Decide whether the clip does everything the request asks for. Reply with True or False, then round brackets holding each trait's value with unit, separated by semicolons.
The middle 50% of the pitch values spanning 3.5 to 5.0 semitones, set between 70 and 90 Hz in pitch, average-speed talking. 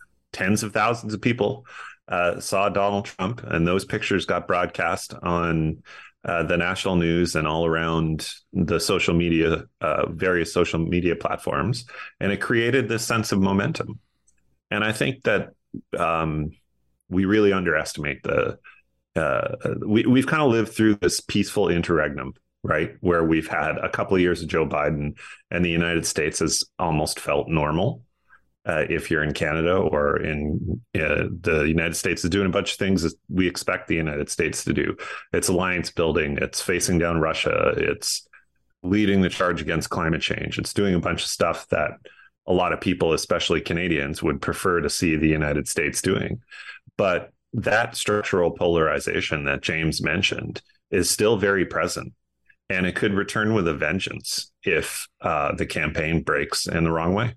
True (3.9 semitones; 85 Hz; 170 wpm)